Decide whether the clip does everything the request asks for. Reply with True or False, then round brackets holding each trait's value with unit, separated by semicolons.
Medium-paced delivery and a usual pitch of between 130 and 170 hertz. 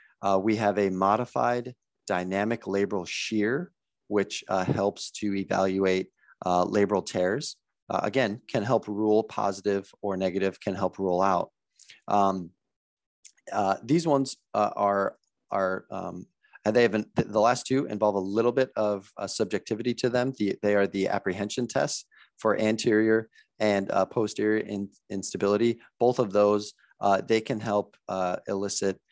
False (155 wpm; 105 Hz)